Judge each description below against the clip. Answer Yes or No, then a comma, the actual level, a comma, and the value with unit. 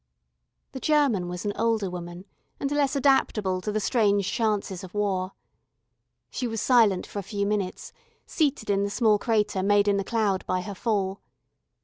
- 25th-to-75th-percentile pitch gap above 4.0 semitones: No, average, 2.9 semitones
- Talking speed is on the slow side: No, average, 170 wpm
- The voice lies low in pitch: No, high, 205 Hz